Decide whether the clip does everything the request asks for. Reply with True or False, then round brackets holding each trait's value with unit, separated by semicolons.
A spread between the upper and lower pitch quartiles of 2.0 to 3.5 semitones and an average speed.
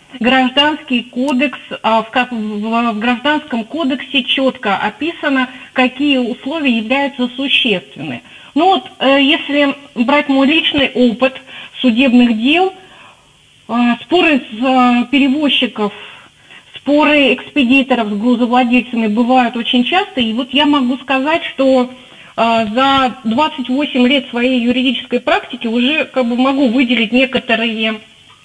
False (2.5 semitones; 100 wpm)